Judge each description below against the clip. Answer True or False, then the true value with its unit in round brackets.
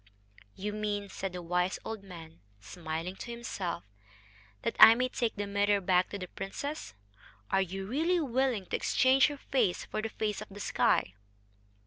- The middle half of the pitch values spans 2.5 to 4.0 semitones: False (4.4 semitones)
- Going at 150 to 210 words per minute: True (170 wpm)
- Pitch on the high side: True (205 Hz)